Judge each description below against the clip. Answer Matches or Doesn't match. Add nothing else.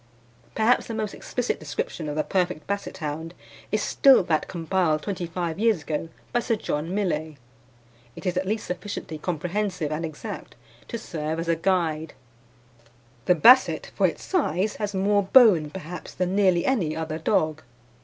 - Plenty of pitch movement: Doesn't match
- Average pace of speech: Matches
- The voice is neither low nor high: Matches